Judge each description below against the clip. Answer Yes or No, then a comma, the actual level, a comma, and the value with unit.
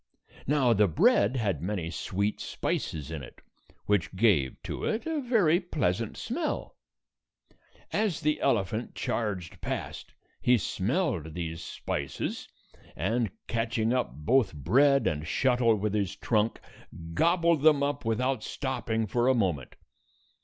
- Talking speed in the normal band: No, slow, 130 wpm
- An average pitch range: No, wide, 6.9 semitones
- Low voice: Yes, low, 115 Hz